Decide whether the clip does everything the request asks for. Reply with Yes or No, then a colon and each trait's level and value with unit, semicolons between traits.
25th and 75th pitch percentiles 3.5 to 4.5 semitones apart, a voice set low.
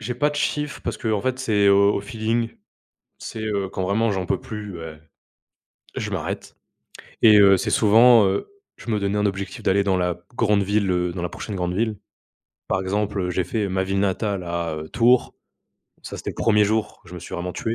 No: average, 2.8 semitones; low, 100 Hz